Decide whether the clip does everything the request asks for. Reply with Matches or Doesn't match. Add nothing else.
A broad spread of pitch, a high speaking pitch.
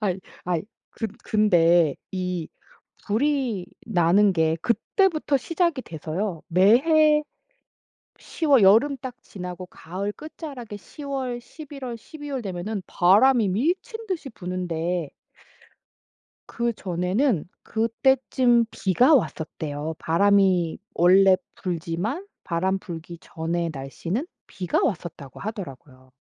Matches